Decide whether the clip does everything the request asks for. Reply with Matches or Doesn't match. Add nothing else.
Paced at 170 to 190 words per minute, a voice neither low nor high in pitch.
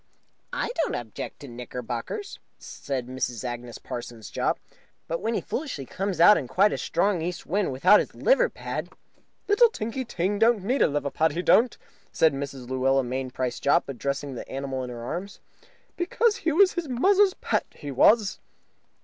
Matches